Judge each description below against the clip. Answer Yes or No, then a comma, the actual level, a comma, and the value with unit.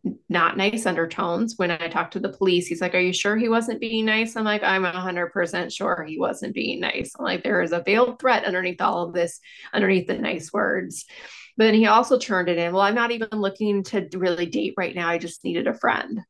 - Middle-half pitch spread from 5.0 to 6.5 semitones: No, average, 3.6 semitones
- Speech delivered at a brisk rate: Yes, fast, 235 wpm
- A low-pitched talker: No, high, 195 Hz